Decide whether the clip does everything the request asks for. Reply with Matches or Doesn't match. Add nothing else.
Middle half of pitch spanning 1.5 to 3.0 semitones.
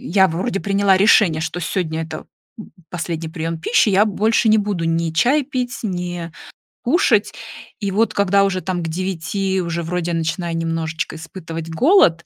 Doesn't match